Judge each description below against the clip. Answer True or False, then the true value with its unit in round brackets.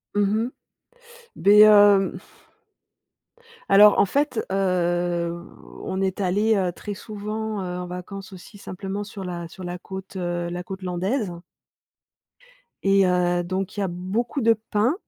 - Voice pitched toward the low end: False (190 Hz)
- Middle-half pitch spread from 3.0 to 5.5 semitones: False (2.5 semitones)